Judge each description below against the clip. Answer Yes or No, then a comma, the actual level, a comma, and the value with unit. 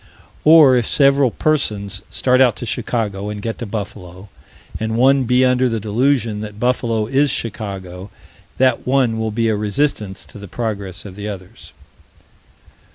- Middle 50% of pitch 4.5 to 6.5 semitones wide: No, average, 3.8 semitones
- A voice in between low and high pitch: No, low, 115 Hz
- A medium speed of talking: Yes, average, 160 wpm